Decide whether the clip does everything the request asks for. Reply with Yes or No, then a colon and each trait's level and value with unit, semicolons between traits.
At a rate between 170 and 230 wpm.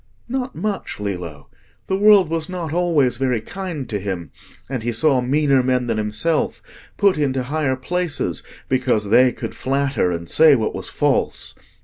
No: average, 160 wpm